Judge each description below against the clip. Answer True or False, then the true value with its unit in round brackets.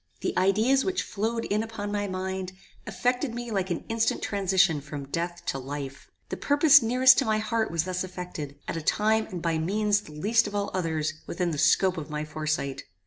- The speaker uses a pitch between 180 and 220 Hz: True (190 Hz)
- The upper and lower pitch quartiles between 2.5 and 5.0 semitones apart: False (5.5 semitones)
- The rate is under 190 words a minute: False (200 wpm)